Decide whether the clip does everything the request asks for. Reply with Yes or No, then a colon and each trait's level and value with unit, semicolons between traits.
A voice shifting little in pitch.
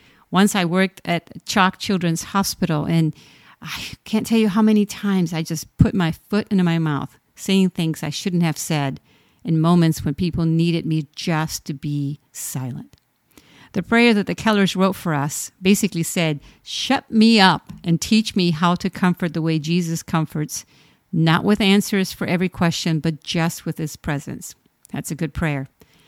No: average, 3.5 semitones